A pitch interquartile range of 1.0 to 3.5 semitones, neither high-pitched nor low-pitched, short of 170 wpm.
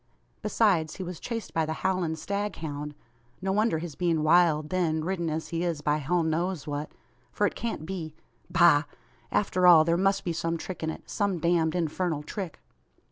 No: average, 2.7 semitones; medium, 170 Hz; average, 185 wpm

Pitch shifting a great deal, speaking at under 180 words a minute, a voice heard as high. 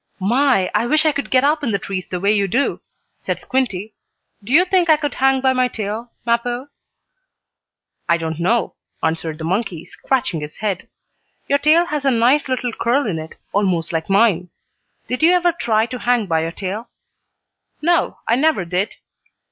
No: wide, 6.4 semitones; average, 185 wpm; high, 235 Hz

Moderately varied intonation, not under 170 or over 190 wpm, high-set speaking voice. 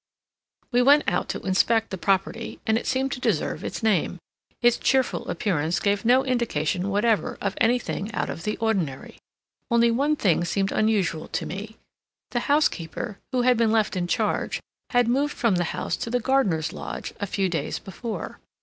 Yes: average, 4.4 semitones; average, 175 wpm; high, 220 Hz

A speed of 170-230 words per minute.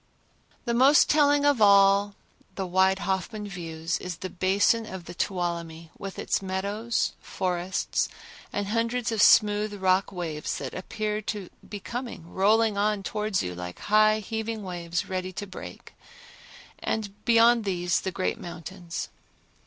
No: average, 145 wpm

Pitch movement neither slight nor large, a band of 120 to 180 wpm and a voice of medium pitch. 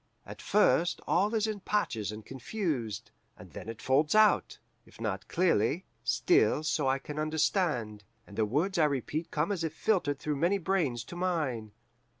No: wide, 7.0 semitones; average, 170 wpm; medium, 155 Hz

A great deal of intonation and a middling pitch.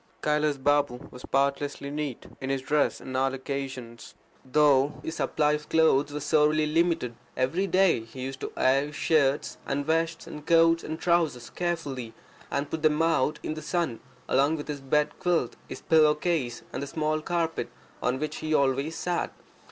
No: average, 3.0 semitones; medium, 150 Hz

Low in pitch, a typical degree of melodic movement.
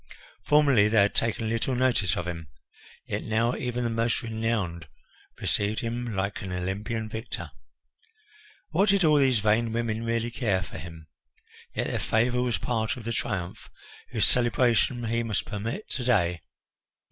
Yes: low, 115 Hz; average, 3.0 semitones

